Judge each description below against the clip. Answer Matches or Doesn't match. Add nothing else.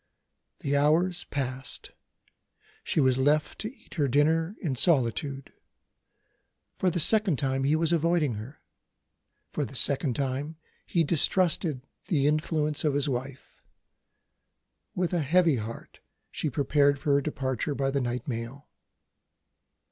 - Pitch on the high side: Doesn't match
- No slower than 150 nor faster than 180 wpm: Doesn't match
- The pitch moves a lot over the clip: Doesn't match